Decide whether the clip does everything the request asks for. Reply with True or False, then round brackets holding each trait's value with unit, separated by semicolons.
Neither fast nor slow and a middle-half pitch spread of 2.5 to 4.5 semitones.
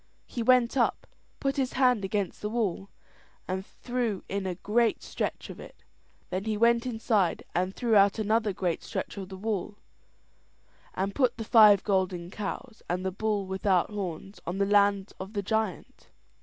True (170 wpm; 3.0 semitones)